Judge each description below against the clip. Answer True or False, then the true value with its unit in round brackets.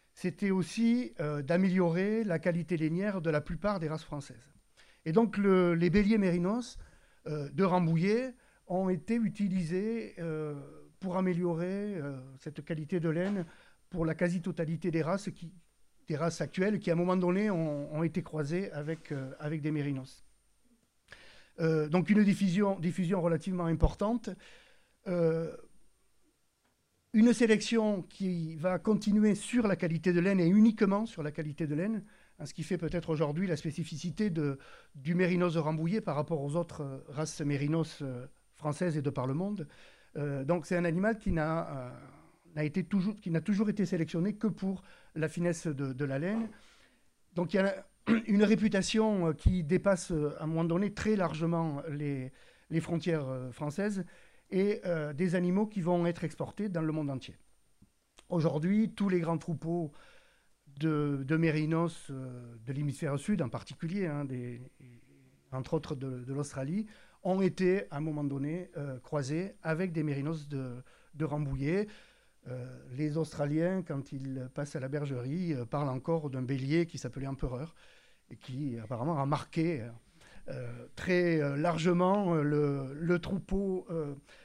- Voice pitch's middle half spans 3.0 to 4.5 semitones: True (4.1 semitones)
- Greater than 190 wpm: False (160 wpm)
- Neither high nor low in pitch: True (165 Hz)